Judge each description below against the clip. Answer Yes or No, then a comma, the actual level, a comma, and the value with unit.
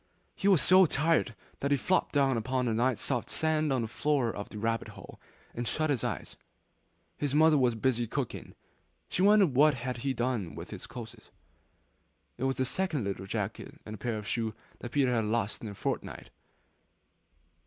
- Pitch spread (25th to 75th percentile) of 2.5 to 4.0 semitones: No, average, 4.5 semitones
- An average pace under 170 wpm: No, average, 185 wpm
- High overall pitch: No, low, 125 Hz